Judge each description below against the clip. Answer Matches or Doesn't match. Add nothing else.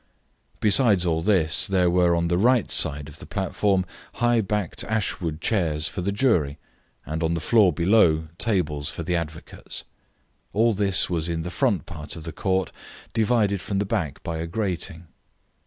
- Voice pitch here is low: Matches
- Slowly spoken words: Doesn't match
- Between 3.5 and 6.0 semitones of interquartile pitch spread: Matches